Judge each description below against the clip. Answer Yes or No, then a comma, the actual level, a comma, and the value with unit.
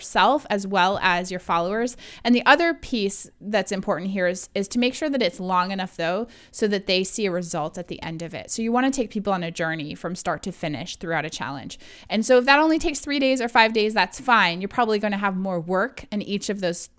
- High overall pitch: Yes, high, 200 Hz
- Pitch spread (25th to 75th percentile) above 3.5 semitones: Yes, average, 4.9 semitones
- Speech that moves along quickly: Yes, fast, 260 wpm